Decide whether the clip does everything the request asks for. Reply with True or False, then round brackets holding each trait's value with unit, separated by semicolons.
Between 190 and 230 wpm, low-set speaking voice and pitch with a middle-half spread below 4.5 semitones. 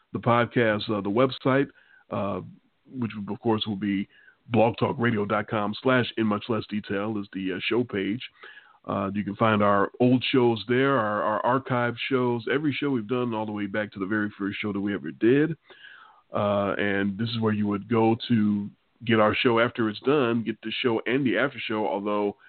True (200 wpm; 110 Hz; 2.8 semitones)